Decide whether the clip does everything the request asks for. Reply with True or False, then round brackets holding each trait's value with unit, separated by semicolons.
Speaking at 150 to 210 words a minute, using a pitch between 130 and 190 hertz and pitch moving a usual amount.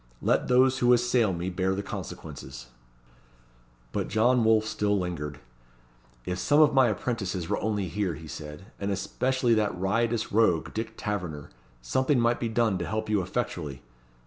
False (160 wpm; 105 Hz; 4.6 semitones)